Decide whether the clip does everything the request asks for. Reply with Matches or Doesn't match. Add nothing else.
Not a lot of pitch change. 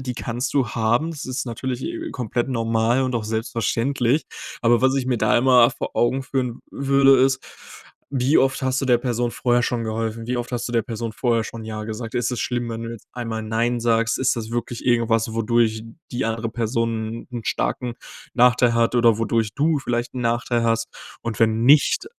Matches